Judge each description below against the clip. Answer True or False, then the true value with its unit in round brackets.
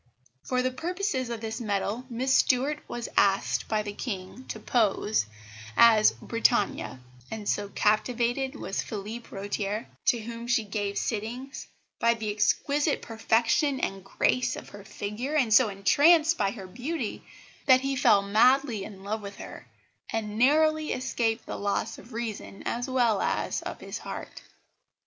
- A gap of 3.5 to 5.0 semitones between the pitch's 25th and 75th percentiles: True (3.8 semitones)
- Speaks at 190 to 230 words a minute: False (155 wpm)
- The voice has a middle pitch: False (230 Hz)